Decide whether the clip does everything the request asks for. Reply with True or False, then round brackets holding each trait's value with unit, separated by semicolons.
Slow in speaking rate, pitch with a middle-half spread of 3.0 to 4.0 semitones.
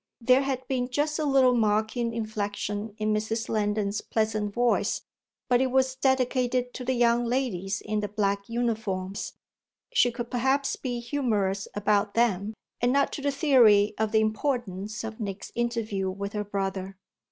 False (160 wpm; 3.3 semitones)